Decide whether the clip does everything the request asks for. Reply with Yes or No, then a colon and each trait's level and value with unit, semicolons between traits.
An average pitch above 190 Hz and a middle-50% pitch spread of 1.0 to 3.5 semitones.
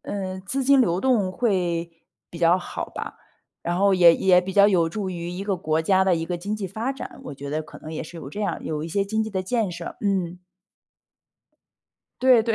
No: medium, 185 Hz; average, 3.2 semitones